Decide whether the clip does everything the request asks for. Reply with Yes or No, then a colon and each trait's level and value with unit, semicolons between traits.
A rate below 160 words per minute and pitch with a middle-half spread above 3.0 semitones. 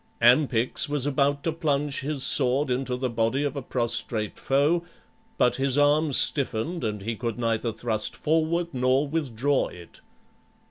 Yes: average, 150 wpm; average, 3.6 semitones